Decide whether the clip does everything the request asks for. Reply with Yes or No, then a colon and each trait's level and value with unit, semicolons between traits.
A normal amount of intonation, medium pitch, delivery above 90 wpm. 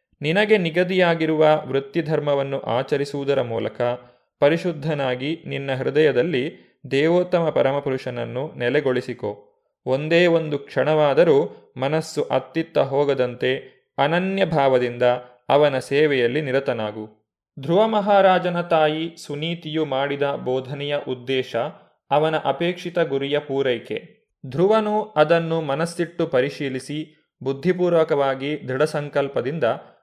No: average, 3.9 semitones; medium, 145 Hz; average, 80 wpm